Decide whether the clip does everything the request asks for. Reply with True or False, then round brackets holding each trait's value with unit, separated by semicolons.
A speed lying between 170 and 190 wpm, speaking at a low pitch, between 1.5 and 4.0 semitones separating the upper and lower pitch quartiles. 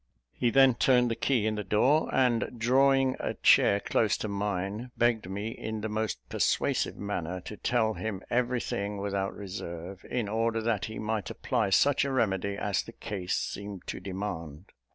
True (175 wpm; 105 Hz; 3.2 semitones)